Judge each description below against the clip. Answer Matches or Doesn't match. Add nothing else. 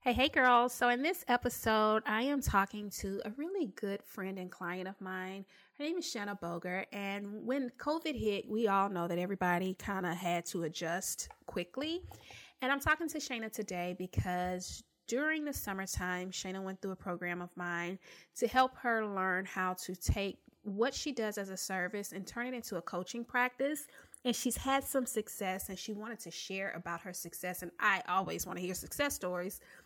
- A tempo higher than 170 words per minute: Matches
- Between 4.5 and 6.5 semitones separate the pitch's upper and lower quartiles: Matches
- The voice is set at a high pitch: Matches